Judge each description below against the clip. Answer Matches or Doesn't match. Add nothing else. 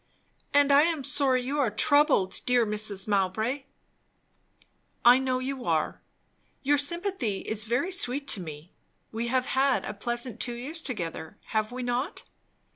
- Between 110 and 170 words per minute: Matches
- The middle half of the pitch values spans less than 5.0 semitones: Matches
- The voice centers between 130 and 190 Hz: Doesn't match